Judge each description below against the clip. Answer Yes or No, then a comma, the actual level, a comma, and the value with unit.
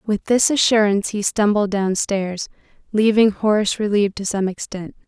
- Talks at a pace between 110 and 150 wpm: Yes, average, 140 wpm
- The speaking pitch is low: No, high, 205 Hz